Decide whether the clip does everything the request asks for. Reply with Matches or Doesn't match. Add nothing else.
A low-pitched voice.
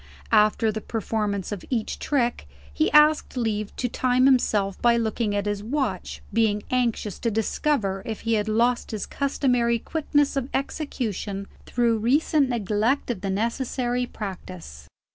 Doesn't match